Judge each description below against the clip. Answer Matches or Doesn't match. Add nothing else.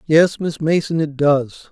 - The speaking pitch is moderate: Matches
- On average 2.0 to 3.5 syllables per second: Doesn't match